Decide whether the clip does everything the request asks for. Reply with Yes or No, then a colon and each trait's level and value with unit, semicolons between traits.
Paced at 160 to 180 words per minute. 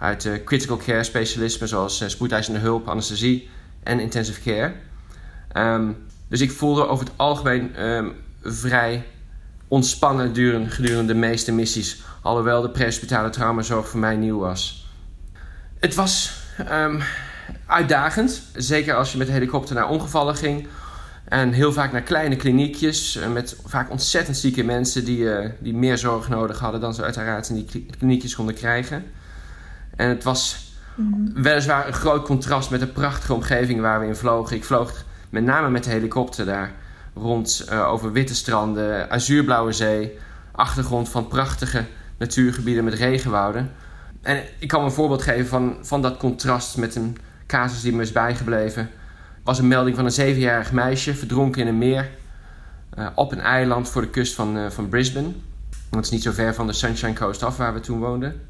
Yes: average, 170 wpm